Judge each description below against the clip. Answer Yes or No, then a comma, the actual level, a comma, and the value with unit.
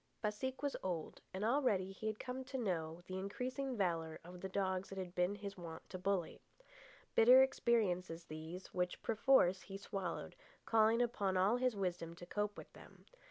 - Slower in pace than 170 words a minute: No, average, 175 wpm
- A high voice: Yes, high, 195 Hz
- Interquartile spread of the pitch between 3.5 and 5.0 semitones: Yes, average, 4.2 semitones